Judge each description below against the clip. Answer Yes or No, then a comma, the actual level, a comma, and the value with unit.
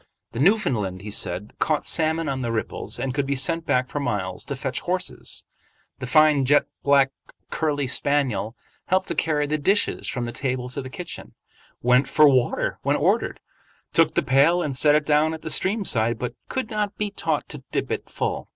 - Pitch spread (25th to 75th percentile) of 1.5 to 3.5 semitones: No, average, 4.0 semitones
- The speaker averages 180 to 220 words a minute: Yes, average, 195 wpm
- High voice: No, medium, 140 Hz